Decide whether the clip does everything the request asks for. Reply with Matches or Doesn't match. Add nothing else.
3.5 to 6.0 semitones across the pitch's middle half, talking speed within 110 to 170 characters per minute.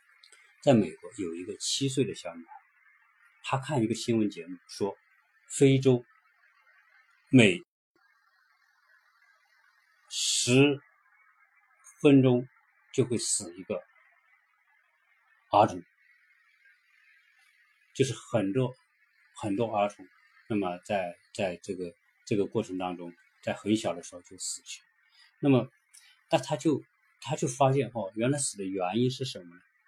Matches